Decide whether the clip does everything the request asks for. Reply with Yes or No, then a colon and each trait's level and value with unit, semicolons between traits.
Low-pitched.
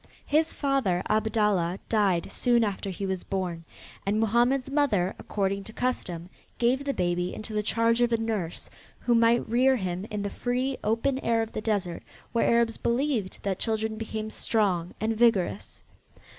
No: high, 220 Hz